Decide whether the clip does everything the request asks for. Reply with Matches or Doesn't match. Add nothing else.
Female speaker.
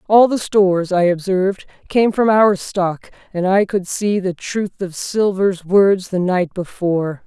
Matches